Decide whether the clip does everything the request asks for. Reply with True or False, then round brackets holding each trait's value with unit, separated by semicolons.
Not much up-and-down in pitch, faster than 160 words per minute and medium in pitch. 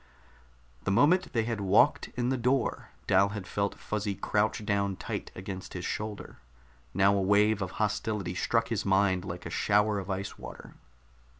False (2.0 semitones; 170 wpm; 100 Hz)